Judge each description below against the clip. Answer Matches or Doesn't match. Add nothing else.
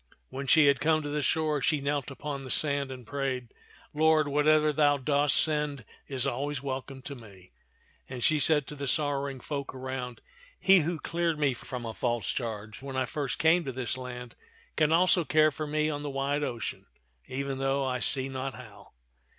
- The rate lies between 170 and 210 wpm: Matches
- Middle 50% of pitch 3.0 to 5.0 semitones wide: Doesn't match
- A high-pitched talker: Doesn't match